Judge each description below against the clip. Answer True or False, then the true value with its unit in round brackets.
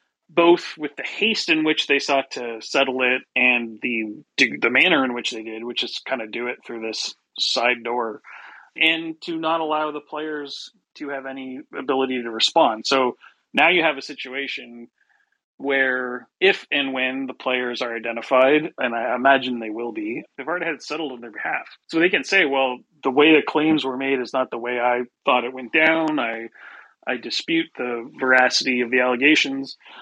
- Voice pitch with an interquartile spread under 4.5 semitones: True (3.7 semitones)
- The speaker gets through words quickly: False (195 wpm)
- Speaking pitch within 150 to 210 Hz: False (130 Hz)